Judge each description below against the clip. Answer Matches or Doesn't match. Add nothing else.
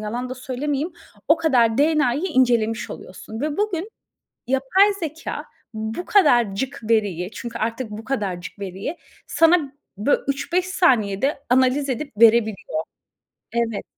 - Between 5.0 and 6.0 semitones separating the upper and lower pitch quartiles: Matches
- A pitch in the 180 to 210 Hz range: Doesn't match